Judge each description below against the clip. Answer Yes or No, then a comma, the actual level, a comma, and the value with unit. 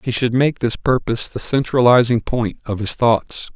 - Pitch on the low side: Yes, low, 120 Hz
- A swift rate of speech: No, average, 185 wpm